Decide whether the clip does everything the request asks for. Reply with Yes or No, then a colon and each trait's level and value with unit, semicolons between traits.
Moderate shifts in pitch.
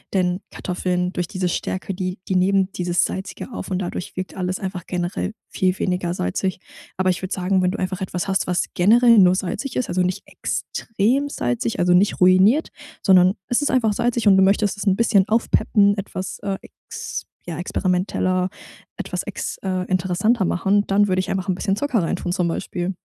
No: narrow, 1.9 semitones